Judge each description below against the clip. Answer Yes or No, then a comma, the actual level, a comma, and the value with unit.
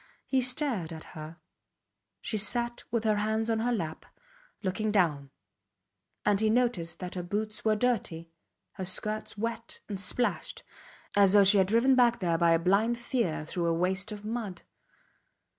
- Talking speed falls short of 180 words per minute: Yes, average, 170 wpm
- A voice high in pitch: Yes, high, 210 Hz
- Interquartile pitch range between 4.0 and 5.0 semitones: Yes, average, 4.3 semitones